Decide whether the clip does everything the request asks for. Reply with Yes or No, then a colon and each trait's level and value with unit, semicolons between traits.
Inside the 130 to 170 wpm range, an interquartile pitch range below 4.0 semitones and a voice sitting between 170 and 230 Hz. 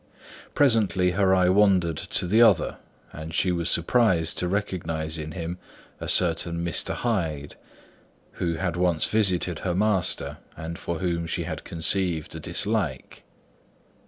No: average, 140 wpm; average, 2.7 semitones; very low, 90 Hz